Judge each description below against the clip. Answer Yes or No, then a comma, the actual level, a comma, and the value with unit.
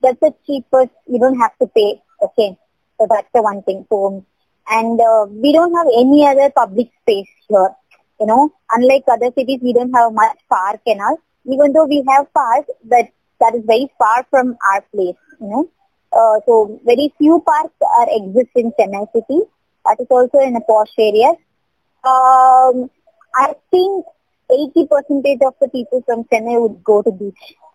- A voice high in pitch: Yes, very high, 250 Hz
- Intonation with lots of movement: No, average, 4.4 semitones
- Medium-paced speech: Yes, average, 175 wpm